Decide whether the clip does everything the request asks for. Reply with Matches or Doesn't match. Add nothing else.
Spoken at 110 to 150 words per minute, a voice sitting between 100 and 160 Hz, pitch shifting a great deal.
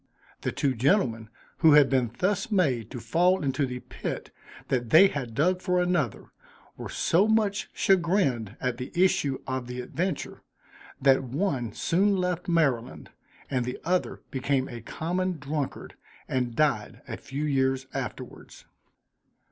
Matches